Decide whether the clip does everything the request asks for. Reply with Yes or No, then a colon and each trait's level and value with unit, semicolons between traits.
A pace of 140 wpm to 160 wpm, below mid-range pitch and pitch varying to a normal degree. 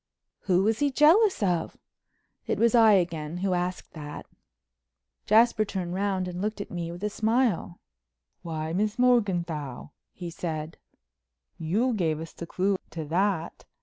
No: average, 150 wpm; medium, 185 Hz; average, 4.4 semitones